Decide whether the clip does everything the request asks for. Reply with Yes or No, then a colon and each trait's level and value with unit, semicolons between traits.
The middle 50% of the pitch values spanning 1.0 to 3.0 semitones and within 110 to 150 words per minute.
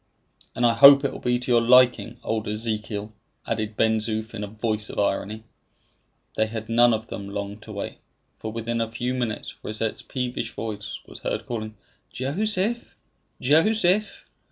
No: narrow, 2.5 semitones; average, 165 wpm